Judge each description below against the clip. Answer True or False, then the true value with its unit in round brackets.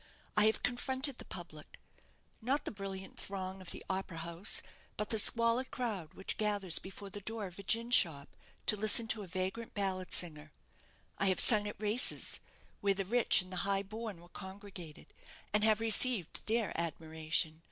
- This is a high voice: True (200 Hz)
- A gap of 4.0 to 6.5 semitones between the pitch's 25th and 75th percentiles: False (3.1 semitones)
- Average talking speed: True (175 wpm)